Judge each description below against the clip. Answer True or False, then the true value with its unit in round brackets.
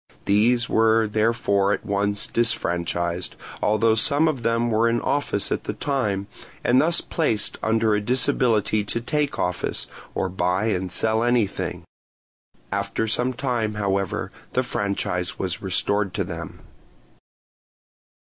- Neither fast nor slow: False (130 wpm)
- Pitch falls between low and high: False (110 Hz)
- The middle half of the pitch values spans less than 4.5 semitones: True (3.2 semitones)